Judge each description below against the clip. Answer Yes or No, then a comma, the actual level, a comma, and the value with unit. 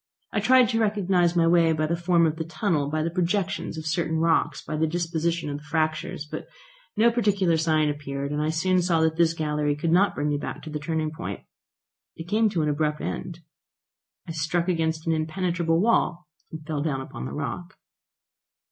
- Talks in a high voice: No, medium, 165 Hz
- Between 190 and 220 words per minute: Yes, average, 200 wpm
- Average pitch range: No, narrow, 2.2 semitones